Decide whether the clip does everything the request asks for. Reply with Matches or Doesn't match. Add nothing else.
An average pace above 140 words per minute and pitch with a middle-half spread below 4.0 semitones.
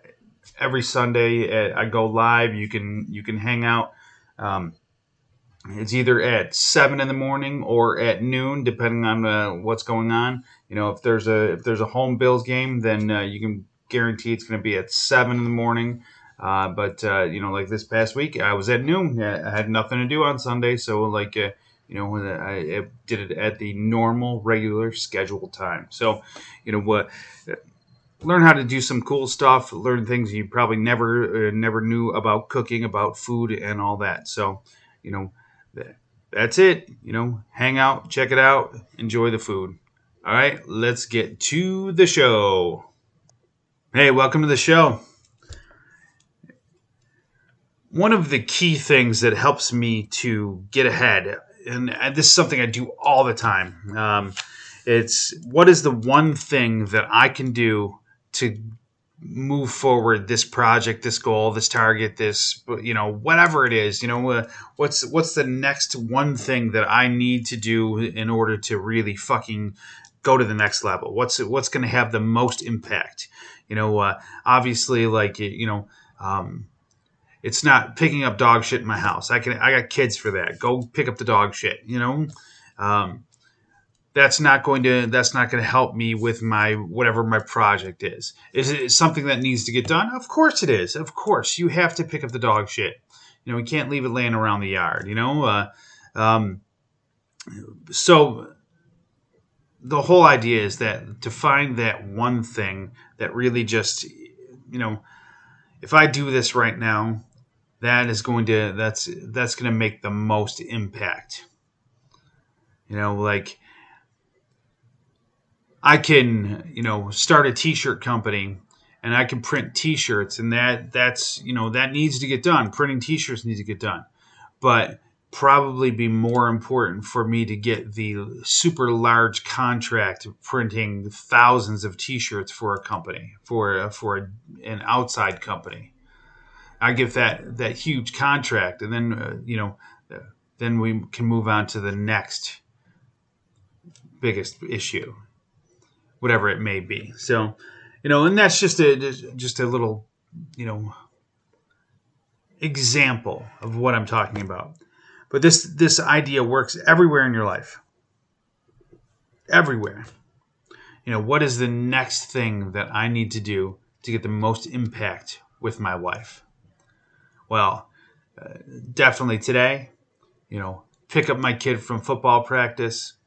Matches